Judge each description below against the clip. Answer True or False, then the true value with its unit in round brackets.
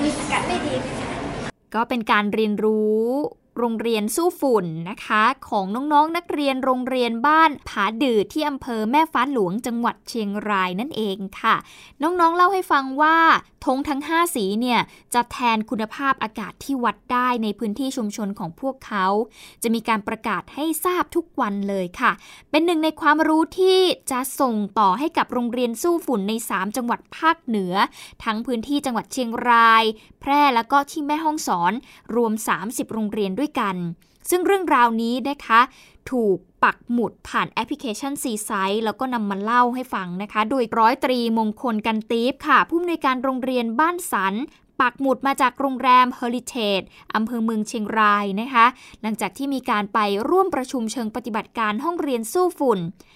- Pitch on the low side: False (240 Hz)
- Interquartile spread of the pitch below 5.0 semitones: True (4.5 semitones)